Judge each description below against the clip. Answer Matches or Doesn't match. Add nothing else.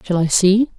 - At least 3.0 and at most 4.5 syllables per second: Doesn't match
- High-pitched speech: Matches